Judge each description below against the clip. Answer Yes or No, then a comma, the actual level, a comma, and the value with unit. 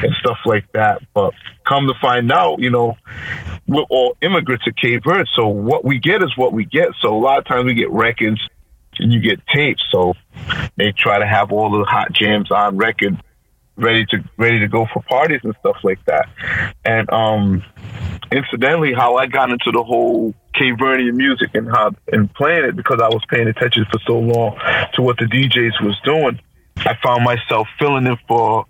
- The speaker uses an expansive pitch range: No, average, 3.0 semitones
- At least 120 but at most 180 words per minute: No, average, 200 wpm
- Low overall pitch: Yes, low, 115 Hz